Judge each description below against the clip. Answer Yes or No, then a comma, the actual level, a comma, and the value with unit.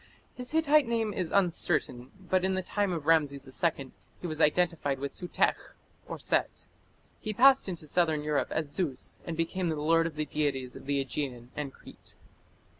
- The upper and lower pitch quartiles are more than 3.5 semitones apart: Yes, average, 4.7 semitones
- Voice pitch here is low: No, medium, 160 Hz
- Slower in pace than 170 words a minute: No, average, 175 wpm